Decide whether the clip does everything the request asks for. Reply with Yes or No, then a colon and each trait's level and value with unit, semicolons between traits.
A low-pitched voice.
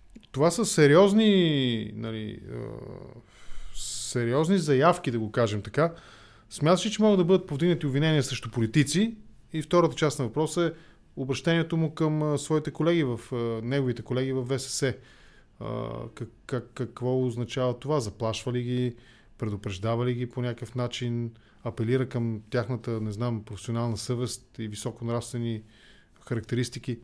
Yes: low, 125 Hz